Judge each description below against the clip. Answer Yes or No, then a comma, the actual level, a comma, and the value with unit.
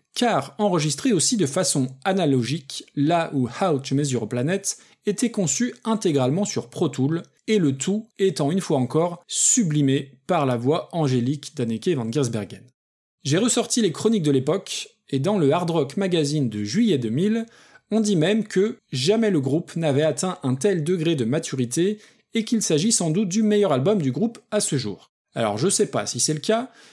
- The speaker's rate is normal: Yes, average, 185 wpm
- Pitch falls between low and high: Yes, medium, 170 Hz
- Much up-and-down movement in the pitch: Yes, wide, 7.2 semitones